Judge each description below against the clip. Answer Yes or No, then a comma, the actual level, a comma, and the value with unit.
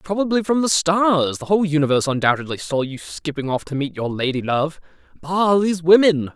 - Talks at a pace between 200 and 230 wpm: No, average, 180 wpm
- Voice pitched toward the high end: No, medium, 160 Hz